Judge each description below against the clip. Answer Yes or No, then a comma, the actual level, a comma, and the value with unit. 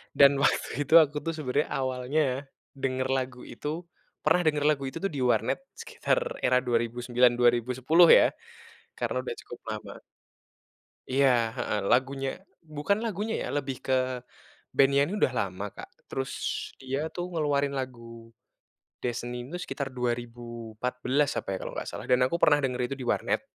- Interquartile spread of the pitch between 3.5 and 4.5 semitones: No, average, 3.0 semitones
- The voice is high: No, low, 130 Hz